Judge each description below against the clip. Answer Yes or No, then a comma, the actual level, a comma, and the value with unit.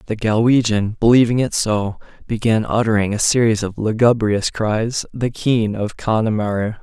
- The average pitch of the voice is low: Yes, low, 110 Hz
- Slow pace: Yes, slow, 130 wpm